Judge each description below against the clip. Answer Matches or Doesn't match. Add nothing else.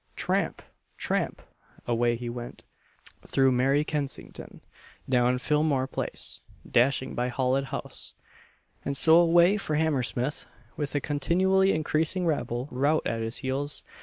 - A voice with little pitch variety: Doesn't match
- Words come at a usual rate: Doesn't match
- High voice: Doesn't match